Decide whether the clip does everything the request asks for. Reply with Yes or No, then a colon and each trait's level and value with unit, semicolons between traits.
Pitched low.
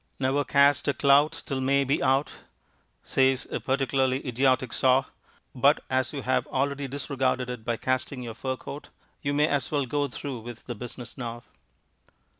Yes: low, 130 Hz